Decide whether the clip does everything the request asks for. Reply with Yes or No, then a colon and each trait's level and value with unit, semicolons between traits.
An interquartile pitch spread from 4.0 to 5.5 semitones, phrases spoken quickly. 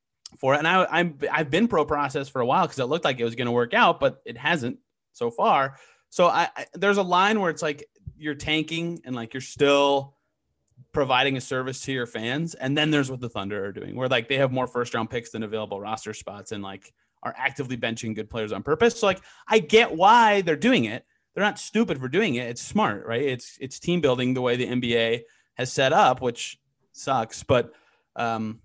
Yes: average, 4.5 semitones; fast, 230 wpm